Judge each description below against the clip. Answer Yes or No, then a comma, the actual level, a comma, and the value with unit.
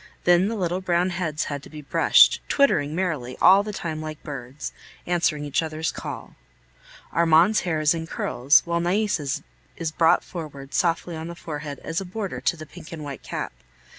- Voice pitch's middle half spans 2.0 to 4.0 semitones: Yes, average, 2.8 semitones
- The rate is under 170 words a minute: No, average, 185 wpm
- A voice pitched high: No, medium, 165 Hz